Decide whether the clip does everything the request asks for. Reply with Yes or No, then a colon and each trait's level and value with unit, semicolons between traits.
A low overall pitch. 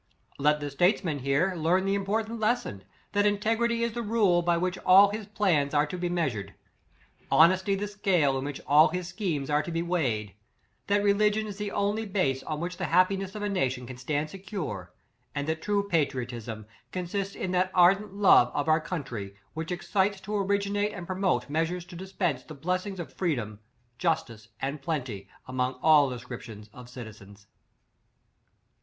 No: medium, 175 Hz